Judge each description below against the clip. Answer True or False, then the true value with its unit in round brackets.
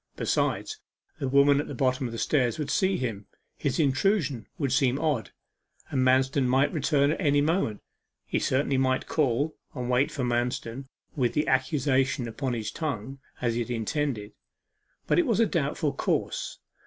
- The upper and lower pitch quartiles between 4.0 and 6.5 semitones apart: False (2.9 semitones)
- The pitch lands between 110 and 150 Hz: True (135 Hz)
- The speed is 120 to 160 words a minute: False (170 wpm)